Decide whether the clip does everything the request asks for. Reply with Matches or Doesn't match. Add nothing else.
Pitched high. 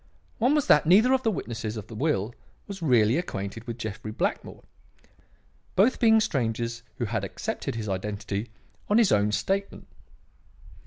Doesn't match